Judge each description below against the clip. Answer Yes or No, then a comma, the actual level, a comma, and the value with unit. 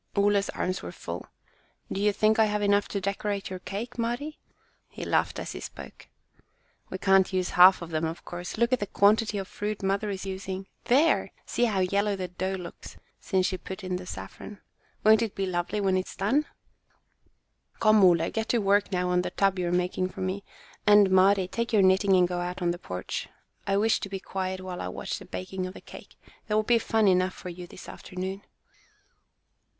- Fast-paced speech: Yes, fast, 210 wpm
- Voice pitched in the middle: No, high, 195 Hz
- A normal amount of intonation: No, narrow, 2.1 semitones